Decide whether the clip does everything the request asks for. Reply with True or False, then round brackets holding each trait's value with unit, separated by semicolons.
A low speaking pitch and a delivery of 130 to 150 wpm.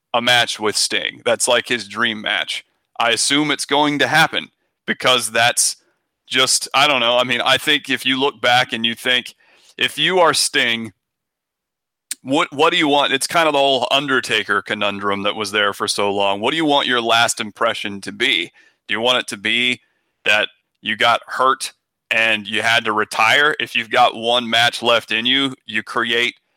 False (120 Hz; 200 wpm)